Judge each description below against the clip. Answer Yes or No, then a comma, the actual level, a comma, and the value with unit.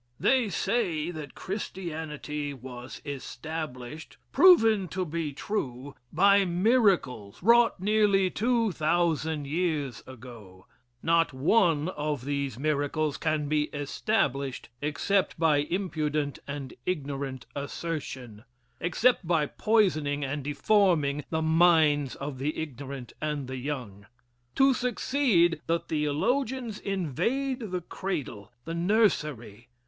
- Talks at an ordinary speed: No, slow, 110 wpm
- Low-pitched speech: No, medium, 155 Hz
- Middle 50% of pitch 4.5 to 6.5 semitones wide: Yes, average, 5.1 semitones